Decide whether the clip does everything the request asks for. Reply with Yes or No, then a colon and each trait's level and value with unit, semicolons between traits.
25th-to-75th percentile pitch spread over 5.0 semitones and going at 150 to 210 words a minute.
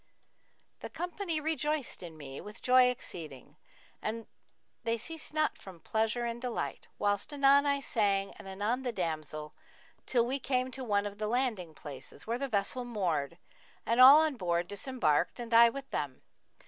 Yes: wide, 5.5 semitones; average, 165 wpm